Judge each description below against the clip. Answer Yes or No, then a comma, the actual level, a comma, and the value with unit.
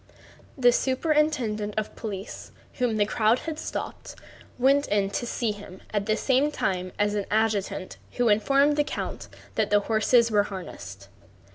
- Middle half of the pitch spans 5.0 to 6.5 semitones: No, average, 3.8 semitones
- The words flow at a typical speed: Yes, average, 155 wpm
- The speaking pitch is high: Yes, high, 215 Hz